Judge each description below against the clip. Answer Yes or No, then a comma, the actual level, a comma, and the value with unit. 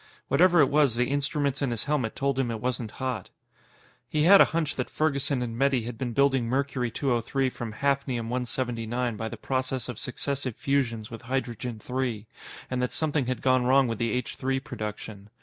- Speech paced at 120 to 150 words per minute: No, average, 190 wpm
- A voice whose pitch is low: Yes, low, 130 Hz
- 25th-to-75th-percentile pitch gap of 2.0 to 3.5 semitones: Yes, average, 2.9 semitones